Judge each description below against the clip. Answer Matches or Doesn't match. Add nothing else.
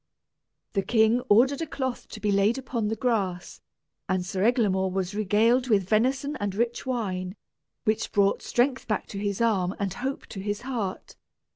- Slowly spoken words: Doesn't match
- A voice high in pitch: Matches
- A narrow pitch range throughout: Doesn't match